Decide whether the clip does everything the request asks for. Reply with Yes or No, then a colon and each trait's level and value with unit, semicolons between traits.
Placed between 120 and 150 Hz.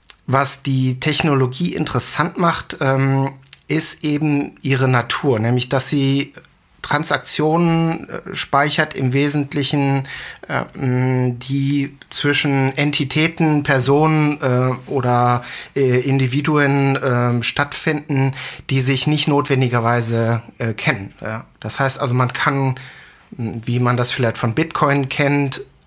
Yes: low, 135 Hz